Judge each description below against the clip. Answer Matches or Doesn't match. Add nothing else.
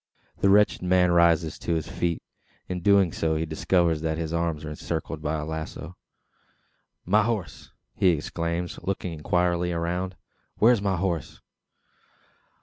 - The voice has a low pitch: Matches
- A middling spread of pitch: Doesn't match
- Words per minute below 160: Matches